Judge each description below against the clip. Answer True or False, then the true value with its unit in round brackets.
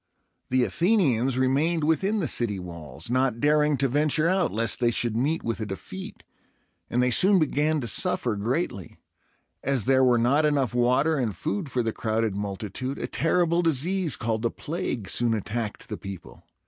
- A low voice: True (130 Hz)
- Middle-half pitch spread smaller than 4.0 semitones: False (5.3 semitones)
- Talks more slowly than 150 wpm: False (175 wpm)